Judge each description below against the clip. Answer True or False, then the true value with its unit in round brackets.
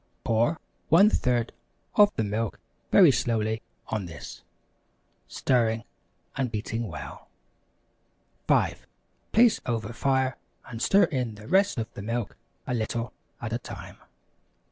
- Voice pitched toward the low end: True (115 Hz)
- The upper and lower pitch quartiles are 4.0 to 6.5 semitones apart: False (2.9 semitones)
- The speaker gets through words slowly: True (120 wpm)